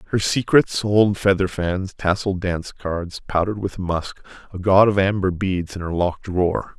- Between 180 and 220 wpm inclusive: No, average, 160 wpm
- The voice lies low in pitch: Yes, very low, 95 Hz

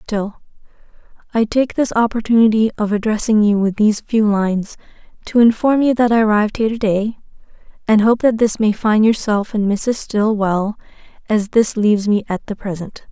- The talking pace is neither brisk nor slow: Yes, average, 175 wpm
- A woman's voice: Yes, female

